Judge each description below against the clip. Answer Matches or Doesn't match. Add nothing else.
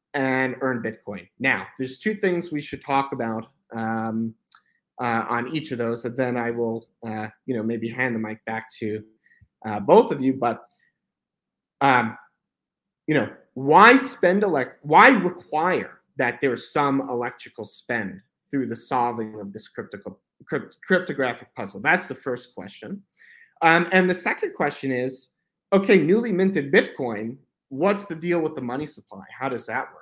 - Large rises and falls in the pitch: Matches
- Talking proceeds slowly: Doesn't match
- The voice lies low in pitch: Matches